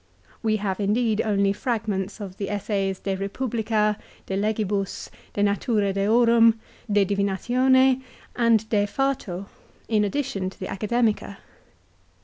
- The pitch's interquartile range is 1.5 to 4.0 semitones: Yes, average, 2.7 semitones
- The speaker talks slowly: No, average, 145 wpm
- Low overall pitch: No, high, 210 Hz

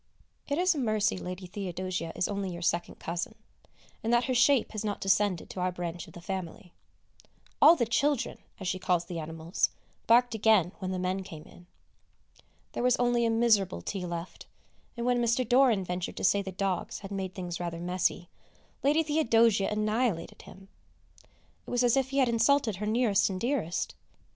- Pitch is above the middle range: Yes, high, 200 Hz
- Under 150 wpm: No, average, 185 wpm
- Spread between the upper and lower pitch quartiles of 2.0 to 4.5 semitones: No, average, 4.9 semitones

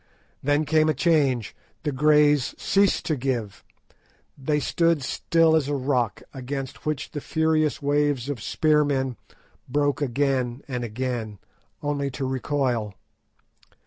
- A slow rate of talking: Yes, slow, 125 wpm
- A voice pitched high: No, medium, 140 Hz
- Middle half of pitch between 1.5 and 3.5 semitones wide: Yes, average, 2.7 semitones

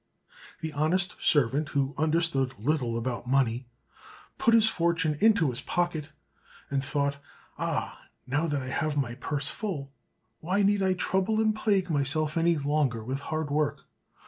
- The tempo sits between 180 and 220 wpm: No, average, 150 wpm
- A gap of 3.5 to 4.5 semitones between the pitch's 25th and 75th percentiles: Yes, average, 4.1 semitones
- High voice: No, medium, 150 Hz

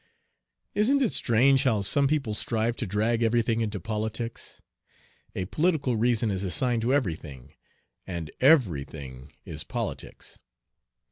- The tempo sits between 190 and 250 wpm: No, slow, 135 wpm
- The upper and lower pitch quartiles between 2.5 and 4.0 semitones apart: No, average, 5.0 semitones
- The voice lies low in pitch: Yes, low, 115 Hz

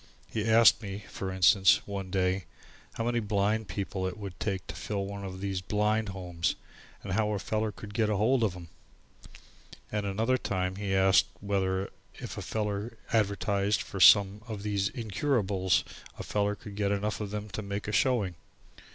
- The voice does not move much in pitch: Yes, narrow, 1.9 semitones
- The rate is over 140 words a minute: Yes, average, 180 wpm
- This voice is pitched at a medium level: No, low, 100 Hz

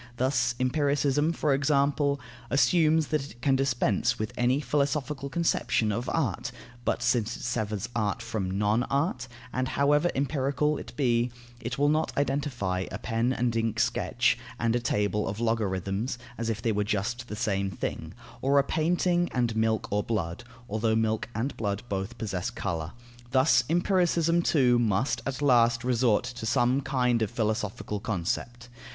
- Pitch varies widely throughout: No, average, 4.3 semitones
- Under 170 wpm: Yes, average, 160 wpm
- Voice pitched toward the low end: Yes, low, 120 Hz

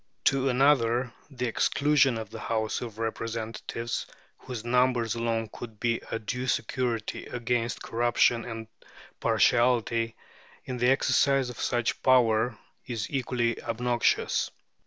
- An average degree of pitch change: No, narrow, 1.7 semitones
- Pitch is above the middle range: No, low, 120 Hz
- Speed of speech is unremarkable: No, slow, 125 wpm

